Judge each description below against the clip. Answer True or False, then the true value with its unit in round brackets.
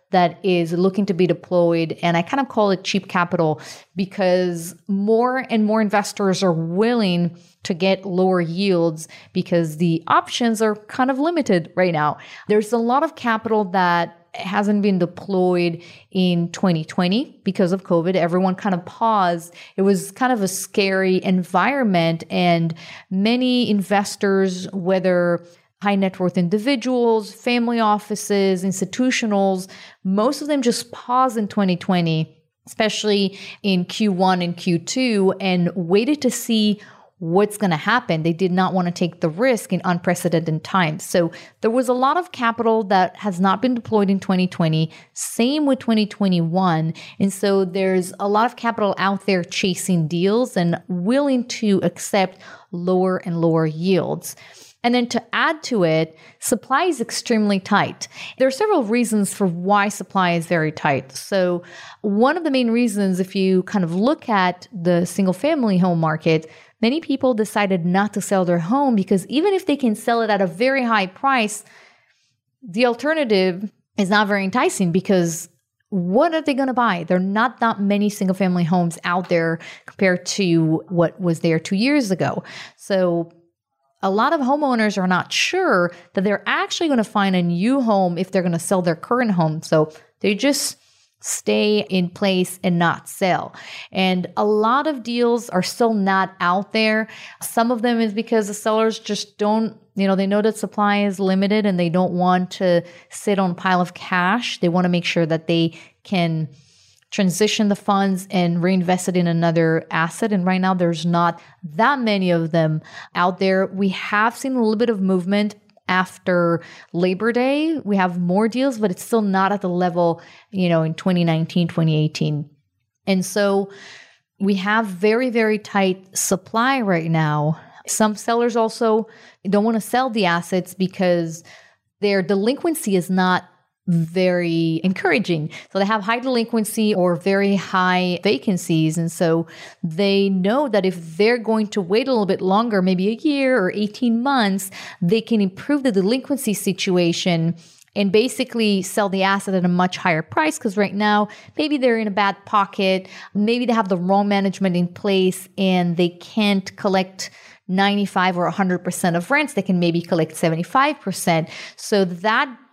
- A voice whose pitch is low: False (195 Hz)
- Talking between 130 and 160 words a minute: False (170 wpm)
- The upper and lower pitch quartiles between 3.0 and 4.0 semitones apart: True (3.7 semitones)